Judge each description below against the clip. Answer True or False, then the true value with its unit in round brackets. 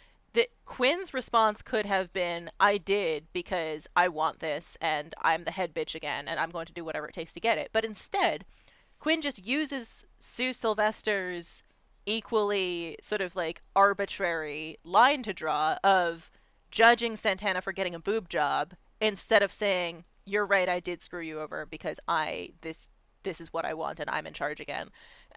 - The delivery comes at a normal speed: True (175 wpm)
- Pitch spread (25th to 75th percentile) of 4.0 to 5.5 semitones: True (4.5 semitones)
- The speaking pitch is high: True (195 Hz)